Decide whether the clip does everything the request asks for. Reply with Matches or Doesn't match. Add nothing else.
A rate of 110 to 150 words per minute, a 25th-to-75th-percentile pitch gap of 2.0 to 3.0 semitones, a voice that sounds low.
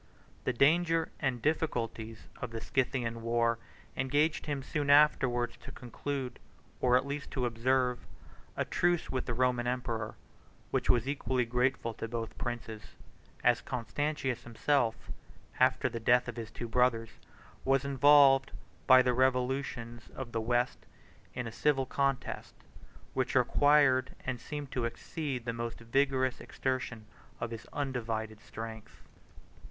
Matches